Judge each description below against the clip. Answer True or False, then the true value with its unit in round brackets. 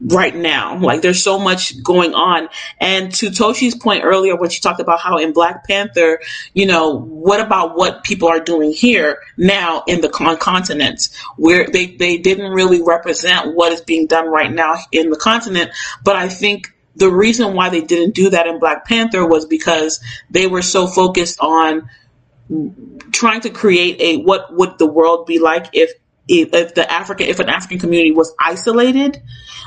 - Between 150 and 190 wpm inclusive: True (180 wpm)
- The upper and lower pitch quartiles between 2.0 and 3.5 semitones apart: True (3.1 semitones)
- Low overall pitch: False (175 Hz)